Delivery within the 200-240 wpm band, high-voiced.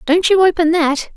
Yes: fast, 205 wpm; very high, 335 Hz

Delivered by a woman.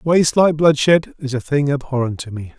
No: male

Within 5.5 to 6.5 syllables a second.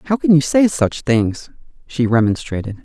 No: 4.8 syllables/s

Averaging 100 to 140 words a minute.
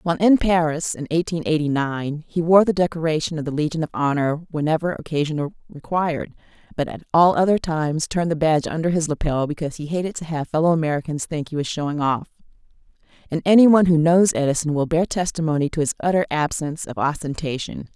No: average, 190 wpm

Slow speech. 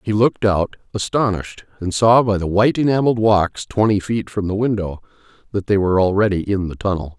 No: average, 190 wpm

